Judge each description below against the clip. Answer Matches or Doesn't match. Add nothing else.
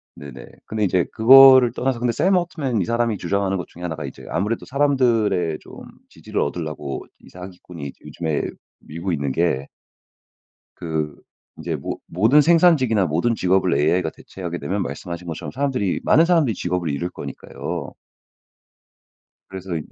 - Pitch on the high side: Doesn't match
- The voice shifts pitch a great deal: Matches